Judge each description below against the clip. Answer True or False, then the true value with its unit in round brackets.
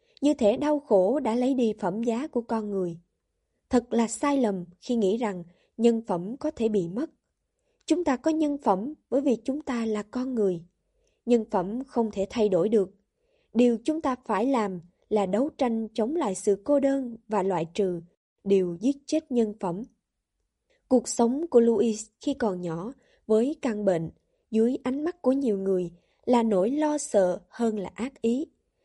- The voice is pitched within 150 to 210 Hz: False (230 Hz)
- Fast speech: False (185 wpm)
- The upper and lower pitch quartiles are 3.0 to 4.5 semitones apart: False (5.1 semitones)